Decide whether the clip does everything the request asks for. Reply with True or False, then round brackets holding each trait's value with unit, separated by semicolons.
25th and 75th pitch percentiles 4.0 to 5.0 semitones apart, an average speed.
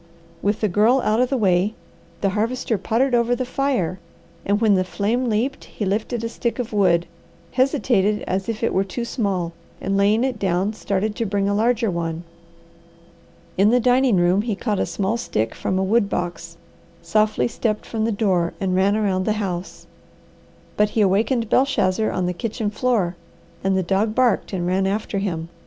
False (3.4 semitones; 185 wpm)